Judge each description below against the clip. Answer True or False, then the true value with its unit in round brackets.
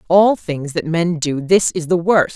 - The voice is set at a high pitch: False (170 Hz)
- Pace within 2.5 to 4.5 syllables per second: True (4.3 syllables/s)